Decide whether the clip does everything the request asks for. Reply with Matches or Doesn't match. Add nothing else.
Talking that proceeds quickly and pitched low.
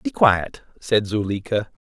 Doesn't match